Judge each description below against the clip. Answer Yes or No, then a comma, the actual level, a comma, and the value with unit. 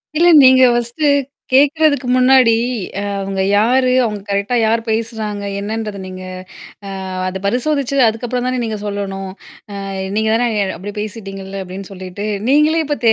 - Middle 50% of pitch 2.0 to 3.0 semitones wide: No, average, 4.3 semitones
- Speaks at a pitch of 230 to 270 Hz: No, high, 220 Hz